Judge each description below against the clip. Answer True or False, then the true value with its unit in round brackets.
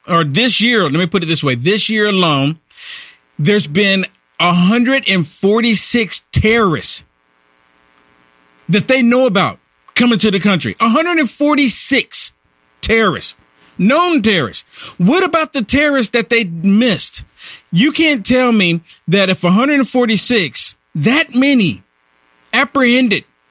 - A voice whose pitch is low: False (200 Hz)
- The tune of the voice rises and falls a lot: True (9.0 semitones)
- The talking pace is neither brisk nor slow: False (115 wpm)